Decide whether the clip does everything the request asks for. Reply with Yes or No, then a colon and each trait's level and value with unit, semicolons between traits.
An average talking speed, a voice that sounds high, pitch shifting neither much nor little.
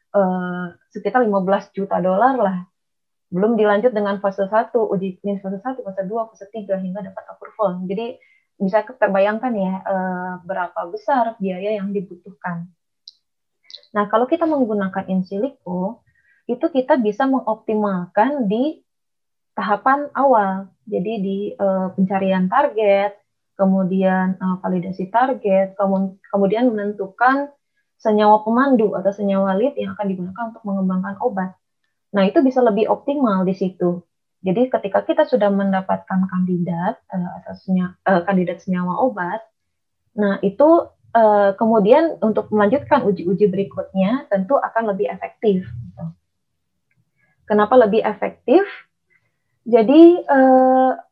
Yes: average, 115 wpm; high, 205 Hz; average, 3.7 semitones